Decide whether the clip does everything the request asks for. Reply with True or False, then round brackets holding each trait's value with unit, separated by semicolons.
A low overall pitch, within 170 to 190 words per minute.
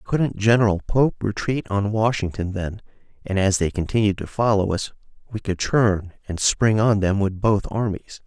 True (105 Hz; 175 wpm)